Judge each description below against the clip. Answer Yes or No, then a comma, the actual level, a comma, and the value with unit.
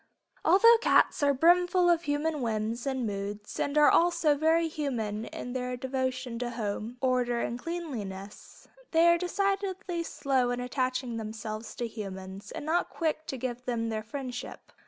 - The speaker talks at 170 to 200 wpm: No, average, 155 wpm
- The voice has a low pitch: No, very high, 255 Hz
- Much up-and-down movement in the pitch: Yes, wide, 5.9 semitones